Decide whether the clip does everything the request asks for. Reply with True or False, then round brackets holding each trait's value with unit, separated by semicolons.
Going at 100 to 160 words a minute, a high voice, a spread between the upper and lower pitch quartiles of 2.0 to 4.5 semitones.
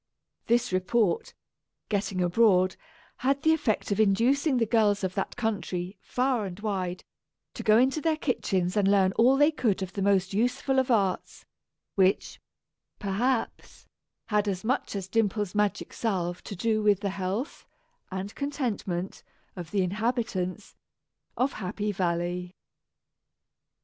True (140 wpm; 205 Hz; 4.2 semitones)